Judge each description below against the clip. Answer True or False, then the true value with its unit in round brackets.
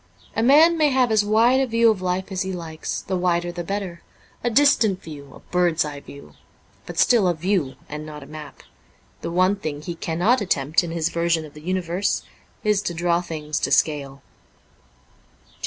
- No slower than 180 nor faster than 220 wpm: True (190 wpm)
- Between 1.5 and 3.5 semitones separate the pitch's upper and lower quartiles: False (4.7 semitones)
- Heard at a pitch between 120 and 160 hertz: False (175 Hz)